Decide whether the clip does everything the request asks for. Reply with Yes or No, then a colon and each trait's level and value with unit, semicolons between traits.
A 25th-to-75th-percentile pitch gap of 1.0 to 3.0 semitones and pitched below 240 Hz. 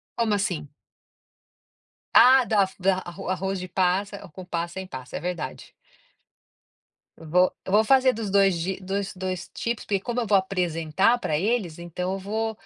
Yes: narrow, 2.6 semitones; high, 190 Hz